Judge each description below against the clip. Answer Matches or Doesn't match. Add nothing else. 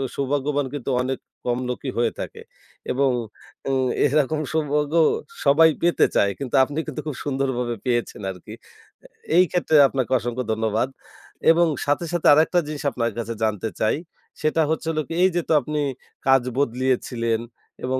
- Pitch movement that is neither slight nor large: Matches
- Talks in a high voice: Doesn't match